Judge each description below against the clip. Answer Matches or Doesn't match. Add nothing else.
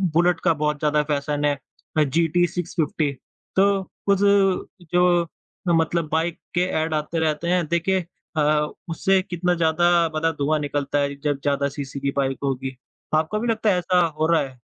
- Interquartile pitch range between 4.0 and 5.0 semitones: Doesn't match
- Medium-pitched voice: Matches